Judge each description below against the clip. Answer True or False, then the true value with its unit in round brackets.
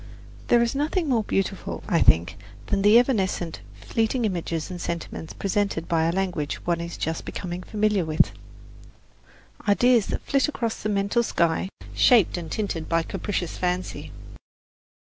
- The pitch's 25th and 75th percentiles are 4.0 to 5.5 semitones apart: True (4.7 semitones)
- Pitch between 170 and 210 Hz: True (190 Hz)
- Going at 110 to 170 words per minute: True (150 wpm)